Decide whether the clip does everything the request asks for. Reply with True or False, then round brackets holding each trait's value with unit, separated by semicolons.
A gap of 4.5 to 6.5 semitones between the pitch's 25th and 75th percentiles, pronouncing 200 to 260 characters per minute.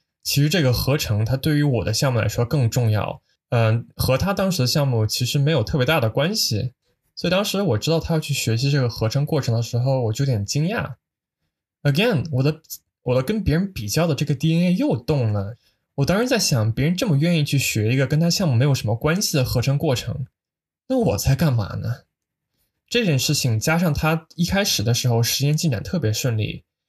False (5.2 semitones; 320 characters per minute)